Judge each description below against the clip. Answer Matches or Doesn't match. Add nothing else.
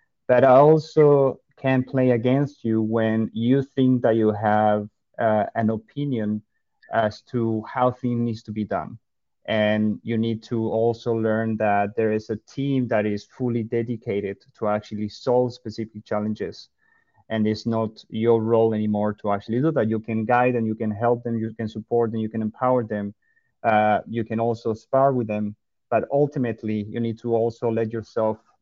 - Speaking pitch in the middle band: Doesn't match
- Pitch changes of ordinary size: Doesn't match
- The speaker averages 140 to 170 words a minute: Doesn't match